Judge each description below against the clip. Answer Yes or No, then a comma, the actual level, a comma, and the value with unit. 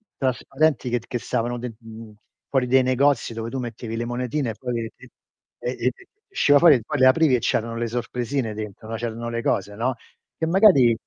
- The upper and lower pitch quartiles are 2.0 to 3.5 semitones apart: Yes, narrow, 2.5 semitones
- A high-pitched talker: No, low, 120 Hz